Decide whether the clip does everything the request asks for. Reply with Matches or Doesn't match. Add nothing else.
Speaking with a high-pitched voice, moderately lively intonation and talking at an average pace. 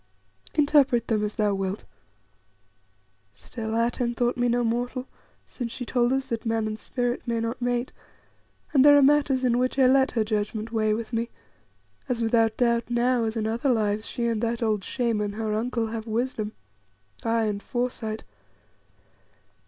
Doesn't match